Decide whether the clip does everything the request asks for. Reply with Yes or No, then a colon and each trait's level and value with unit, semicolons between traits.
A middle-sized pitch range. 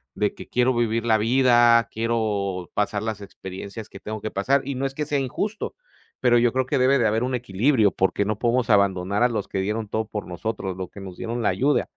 Yes: average, 3.5 semitones